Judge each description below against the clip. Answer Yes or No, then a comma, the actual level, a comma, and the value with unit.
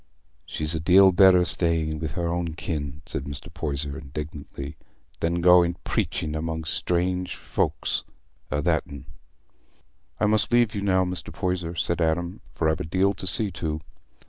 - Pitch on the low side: Yes, very low, 85 Hz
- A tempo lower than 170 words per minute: Yes, average, 160 wpm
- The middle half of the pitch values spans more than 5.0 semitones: No, average, 2.7 semitones